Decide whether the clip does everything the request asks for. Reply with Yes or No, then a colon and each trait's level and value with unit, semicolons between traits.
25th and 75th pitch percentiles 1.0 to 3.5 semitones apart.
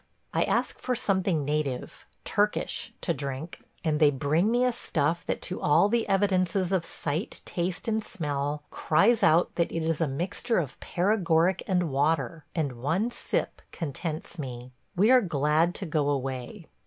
No: average, 4.5 semitones